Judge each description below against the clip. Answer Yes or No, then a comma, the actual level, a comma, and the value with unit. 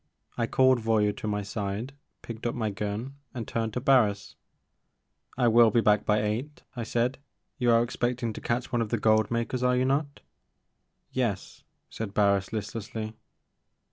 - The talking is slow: No, average, 175 wpm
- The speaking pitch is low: Yes, low, 115 Hz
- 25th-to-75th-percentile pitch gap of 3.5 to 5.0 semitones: No, average, 2.8 semitones